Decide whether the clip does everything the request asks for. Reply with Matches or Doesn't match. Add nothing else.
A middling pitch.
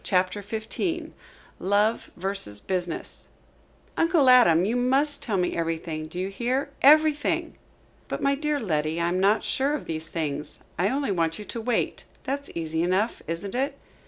Doesn't match